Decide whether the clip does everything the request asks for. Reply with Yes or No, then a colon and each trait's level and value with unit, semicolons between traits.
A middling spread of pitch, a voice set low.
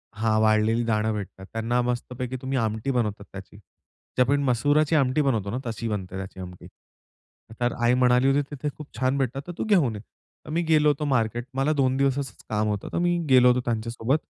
Yes: average, 3.9 semitones; low, 125 Hz